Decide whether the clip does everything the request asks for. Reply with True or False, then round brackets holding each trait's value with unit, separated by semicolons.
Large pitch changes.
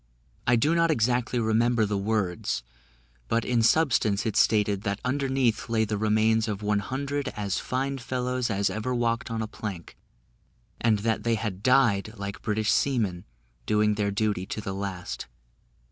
False (3.1 semitones)